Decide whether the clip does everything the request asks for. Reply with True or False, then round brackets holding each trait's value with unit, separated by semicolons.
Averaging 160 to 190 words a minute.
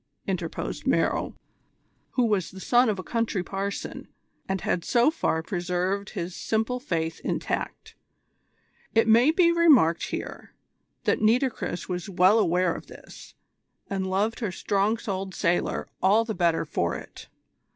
False (140 wpm)